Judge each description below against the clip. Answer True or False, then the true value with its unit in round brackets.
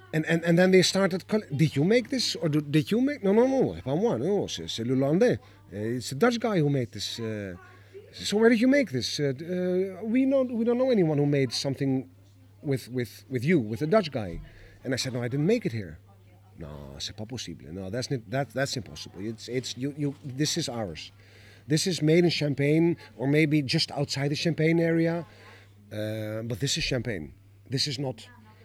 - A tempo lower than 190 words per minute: False (200 wpm)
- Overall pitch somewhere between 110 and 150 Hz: True (135 Hz)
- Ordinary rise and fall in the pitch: False (7.6 semitones)